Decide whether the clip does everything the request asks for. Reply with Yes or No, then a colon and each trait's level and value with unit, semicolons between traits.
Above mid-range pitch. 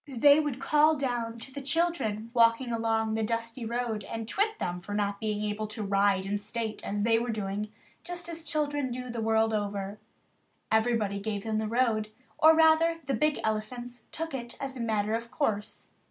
Yes: high, 230 Hz